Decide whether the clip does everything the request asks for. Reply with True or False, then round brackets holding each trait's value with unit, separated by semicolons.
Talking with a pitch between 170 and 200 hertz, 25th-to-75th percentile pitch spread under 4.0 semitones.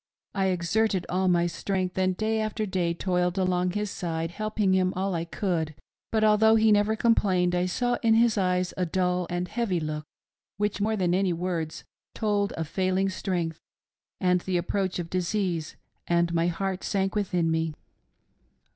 True (185 Hz; 2.8 semitones)